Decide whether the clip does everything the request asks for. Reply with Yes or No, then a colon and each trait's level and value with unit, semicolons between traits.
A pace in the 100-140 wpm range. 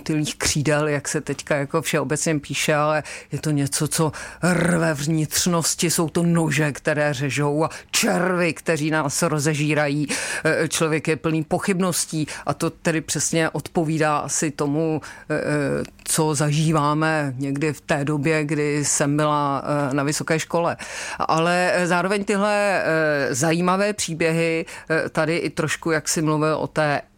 Yes: average, 130 wpm